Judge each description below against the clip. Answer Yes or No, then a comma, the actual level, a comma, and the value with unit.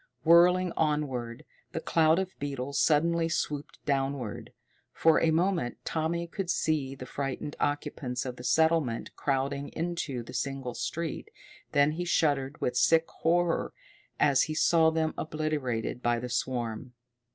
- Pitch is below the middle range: No, medium, 150 Hz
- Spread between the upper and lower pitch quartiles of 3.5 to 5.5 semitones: Yes, average, 3.9 semitones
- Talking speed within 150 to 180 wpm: No, average, 140 wpm